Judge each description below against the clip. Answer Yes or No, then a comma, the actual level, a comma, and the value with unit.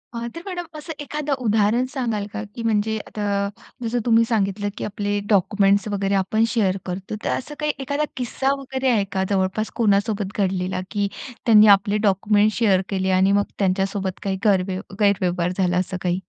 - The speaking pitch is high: Yes, high, 205 Hz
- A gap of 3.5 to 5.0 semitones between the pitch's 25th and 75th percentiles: No, average, 2.9 semitones